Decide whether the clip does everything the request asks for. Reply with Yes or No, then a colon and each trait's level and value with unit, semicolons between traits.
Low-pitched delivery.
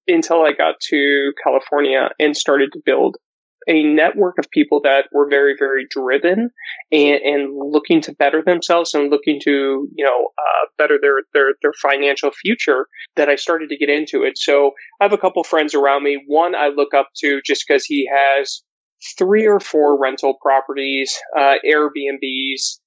No: medium, 145 Hz